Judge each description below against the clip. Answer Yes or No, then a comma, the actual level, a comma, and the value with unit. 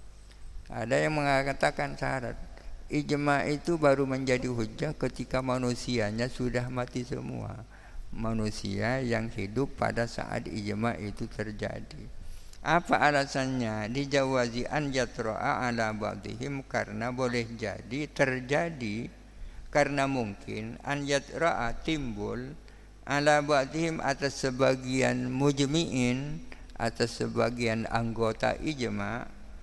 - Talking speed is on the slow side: No, average, 95 wpm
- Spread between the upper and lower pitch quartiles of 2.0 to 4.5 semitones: Yes, average, 3.7 semitones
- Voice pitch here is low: Yes, low, 125 Hz